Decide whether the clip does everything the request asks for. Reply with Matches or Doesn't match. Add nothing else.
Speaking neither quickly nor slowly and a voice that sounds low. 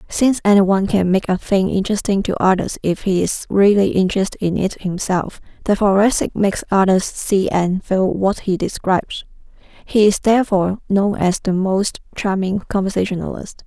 Doesn't match